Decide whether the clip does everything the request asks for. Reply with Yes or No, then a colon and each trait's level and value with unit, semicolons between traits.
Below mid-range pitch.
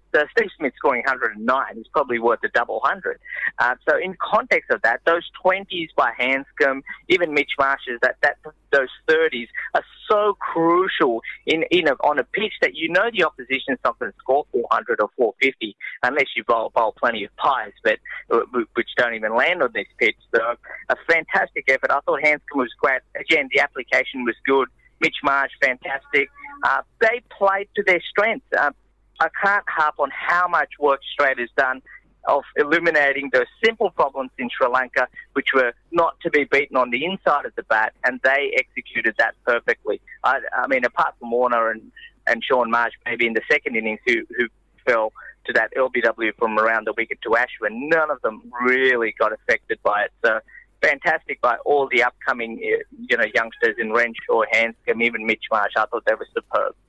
No: medium, 160 Hz